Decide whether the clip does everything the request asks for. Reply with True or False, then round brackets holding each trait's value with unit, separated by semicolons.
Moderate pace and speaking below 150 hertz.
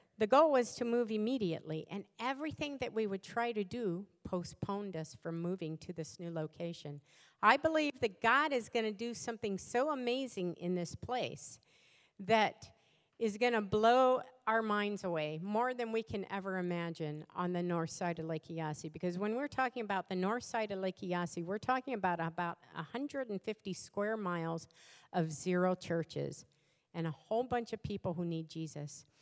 False (180 wpm; 190 Hz)